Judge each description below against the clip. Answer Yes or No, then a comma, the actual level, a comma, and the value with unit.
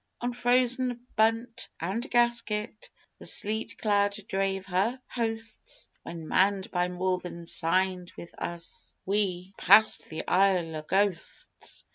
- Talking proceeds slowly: Yes, slow, 125 wpm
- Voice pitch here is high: Yes, high, 195 Hz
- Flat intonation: No, average, 3.9 semitones